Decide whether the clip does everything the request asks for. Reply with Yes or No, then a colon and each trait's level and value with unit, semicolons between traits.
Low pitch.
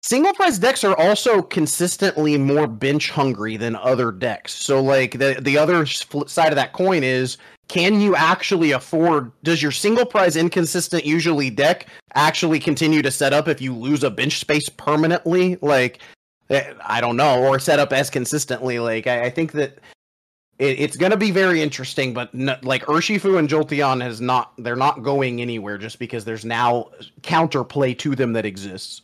No: medium, 145 Hz